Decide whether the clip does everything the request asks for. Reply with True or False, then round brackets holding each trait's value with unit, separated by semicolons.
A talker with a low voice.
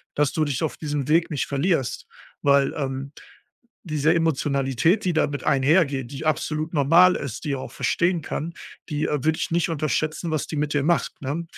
False (150 Hz)